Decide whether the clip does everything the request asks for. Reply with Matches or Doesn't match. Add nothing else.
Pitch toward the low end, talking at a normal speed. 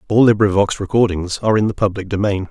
Matches